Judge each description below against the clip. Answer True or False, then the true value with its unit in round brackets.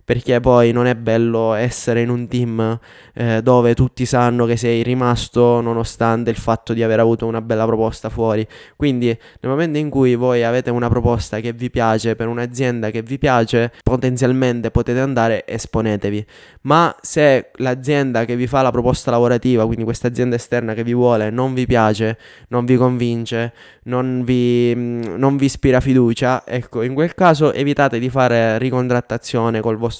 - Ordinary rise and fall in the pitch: False (1.7 semitones)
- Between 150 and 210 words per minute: True (170 wpm)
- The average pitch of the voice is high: False (120 Hz)